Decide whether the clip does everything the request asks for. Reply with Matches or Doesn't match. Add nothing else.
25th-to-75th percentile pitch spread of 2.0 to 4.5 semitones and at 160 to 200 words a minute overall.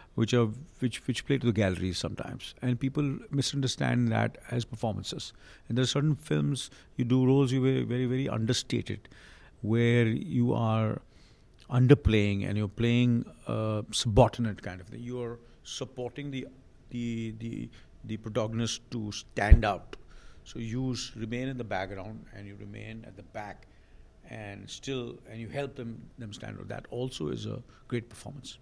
Matches